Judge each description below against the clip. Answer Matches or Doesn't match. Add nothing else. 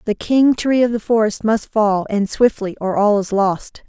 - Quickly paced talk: Matches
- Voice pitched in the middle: Doesn't match